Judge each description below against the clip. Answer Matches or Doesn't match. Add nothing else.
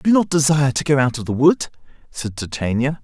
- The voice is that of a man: Matches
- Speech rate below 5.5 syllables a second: Doesn't match